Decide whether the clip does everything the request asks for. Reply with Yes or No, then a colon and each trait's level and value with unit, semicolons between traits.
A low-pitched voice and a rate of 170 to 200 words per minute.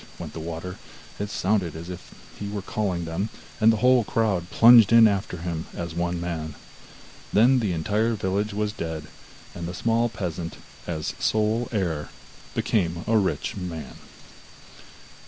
No: very low, 95 Hz; average, 155 wpm